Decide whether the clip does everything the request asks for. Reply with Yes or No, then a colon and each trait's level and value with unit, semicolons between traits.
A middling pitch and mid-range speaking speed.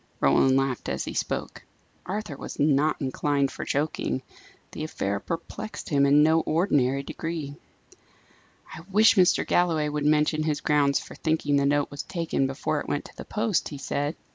Yes: medium, 150 Hz; average, 170 wpm